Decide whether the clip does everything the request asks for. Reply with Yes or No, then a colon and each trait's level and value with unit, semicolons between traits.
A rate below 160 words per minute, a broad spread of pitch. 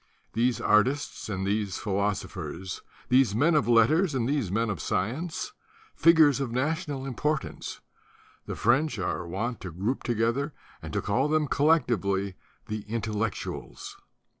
Yes: average, 140 wpm; wide, 5.7 semitones